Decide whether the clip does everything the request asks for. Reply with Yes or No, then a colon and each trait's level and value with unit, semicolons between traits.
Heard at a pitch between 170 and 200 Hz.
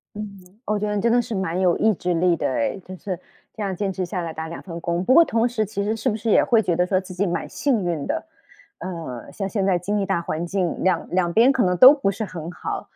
Yes: high, 190 Hz